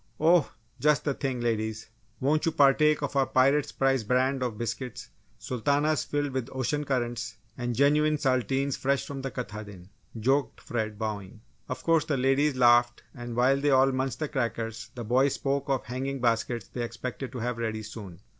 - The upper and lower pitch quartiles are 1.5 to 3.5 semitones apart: Yes, average, 3.1 semitones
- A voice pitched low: Yes, low, 130 Hz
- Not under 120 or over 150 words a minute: No, average, 180 wpm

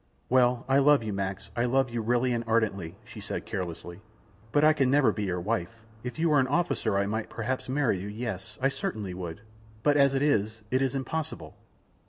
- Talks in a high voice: No, low, 120 Hz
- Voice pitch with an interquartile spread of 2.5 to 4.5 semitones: No, average, 5.1 semitones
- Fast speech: Yes, fast, 210 wpm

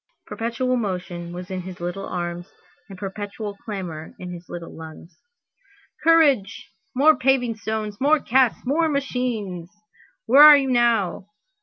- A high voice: Yes, high, 210 Hz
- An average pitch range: No, wide, 6.1 semitones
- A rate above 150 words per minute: No, slow, 135 wpm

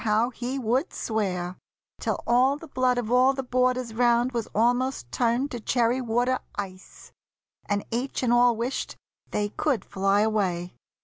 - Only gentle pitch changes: No, average, 3.0 semitones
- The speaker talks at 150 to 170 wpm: Yes, average, 160 wpm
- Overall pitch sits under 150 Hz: No, high, 240 Hz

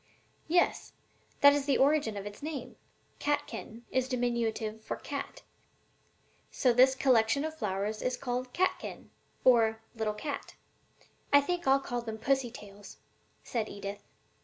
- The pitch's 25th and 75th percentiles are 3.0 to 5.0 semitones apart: Yes, average, 4.1 semitones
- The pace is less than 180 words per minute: Yes, average, 140 wpm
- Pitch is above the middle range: Yes, high, 245 Hz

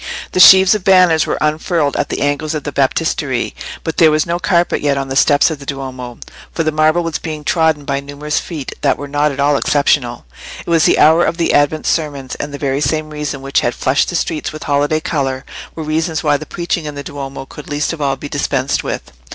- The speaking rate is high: Yes, fast, 235 wpm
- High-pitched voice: No, medium, 150 Hz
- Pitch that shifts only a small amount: Yes, narrow, 2.2 semitones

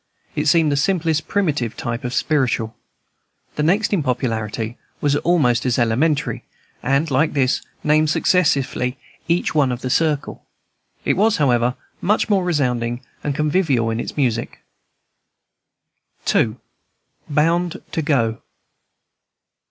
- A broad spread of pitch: No, average, 4.7 semitones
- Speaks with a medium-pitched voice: Yes, medium, 145 Hz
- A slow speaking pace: Yes, slow, 125 wpm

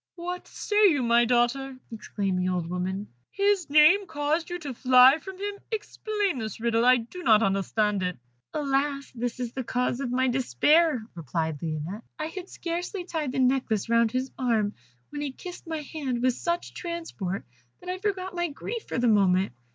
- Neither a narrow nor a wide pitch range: No, wide, 7.3 semitones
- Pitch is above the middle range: Yes, very high, 260 Hz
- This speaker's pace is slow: No, average, 180 wpm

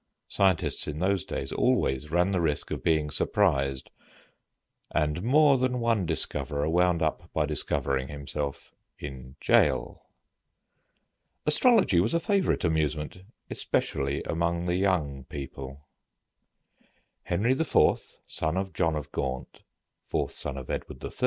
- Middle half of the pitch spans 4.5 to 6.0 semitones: Yes, average, 4.9 semitones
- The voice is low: Yes, very low, 80 Hz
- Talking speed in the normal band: No, slow, 125 wpm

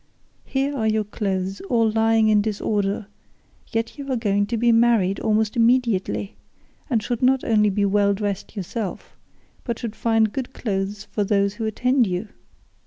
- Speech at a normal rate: Yes, average, 165 wpm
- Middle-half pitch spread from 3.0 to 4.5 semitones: No, narrow, 2.5 semitones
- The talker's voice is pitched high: Yes, high, 220 Hz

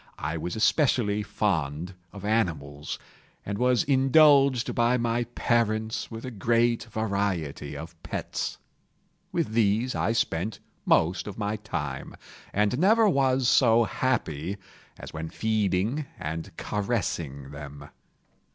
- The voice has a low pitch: Yes, low, 105 Hz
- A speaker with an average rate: No, slow, 120 wpm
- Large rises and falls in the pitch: Yes, wide, 6.4 semitones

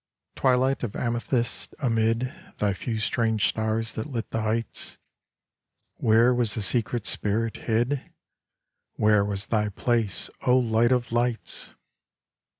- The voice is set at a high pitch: No, low, 115 Hz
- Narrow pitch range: Yes, narrow, 1.9 semitones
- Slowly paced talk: Yes, slow, 125 wpm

